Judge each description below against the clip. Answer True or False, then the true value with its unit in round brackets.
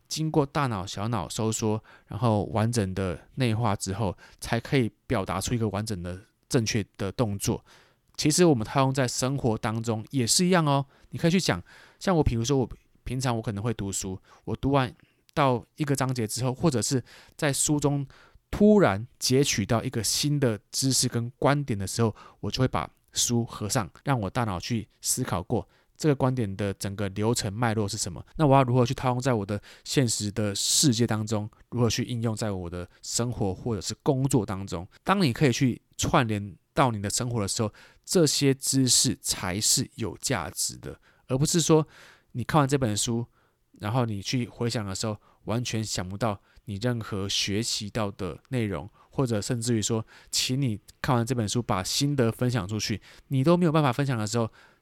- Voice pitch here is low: True (120 Hz)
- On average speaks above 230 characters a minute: True (280 characters per minute)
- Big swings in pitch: False (4.1 semitones)